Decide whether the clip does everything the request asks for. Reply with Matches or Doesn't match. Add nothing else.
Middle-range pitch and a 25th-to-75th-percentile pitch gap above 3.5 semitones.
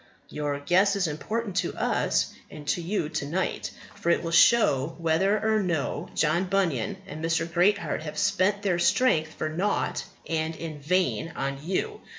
Matches